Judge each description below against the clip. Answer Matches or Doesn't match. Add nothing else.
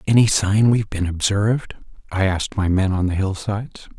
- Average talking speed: Matches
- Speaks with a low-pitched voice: Matches